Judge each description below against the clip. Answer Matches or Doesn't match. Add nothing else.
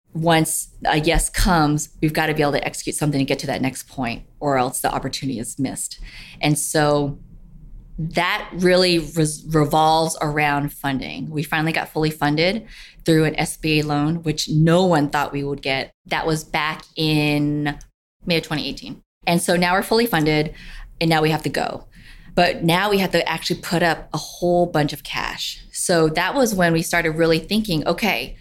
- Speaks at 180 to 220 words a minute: Matches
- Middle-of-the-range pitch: Matches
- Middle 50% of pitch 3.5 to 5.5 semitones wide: Doesn't match